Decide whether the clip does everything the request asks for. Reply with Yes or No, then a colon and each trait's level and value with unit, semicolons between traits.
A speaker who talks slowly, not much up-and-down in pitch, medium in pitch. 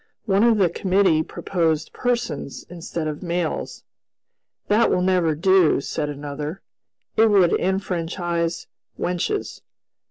No: slow, 115 wpm; average, 3.3 semitones; medium, 175 Hz